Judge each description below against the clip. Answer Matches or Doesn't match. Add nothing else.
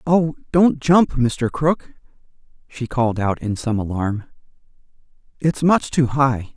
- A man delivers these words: Matches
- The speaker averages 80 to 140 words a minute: Matches